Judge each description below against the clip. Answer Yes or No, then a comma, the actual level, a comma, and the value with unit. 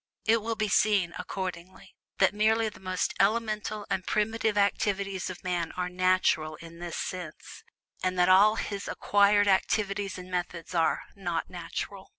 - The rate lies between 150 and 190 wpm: Yes, average, 155 wpm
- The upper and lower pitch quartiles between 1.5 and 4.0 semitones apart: Yes, narrow, 2.5 semitones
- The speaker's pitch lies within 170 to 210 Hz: Yes, high, 190 Hz